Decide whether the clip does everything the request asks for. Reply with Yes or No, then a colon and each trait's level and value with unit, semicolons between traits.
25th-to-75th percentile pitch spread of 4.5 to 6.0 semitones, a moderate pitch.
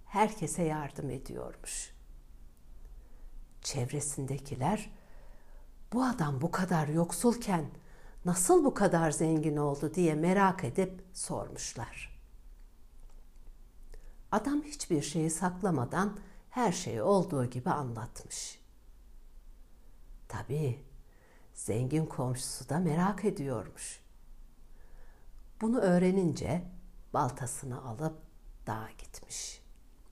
Yes: average, 5.1 semitones; medium, 160 Hz